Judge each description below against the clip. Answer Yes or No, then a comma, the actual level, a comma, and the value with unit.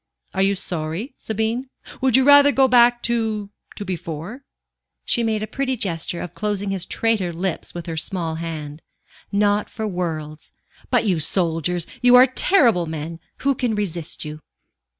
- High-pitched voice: Yes, high, 200 Hz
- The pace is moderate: Yes, average, 160 wpm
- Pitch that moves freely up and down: Yes, wide, 5.9 semitones